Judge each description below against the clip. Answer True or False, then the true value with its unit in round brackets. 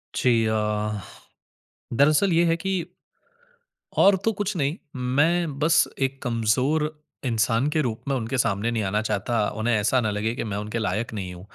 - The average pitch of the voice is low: True (120 Hz)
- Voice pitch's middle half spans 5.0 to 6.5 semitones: True (5.5 semitones)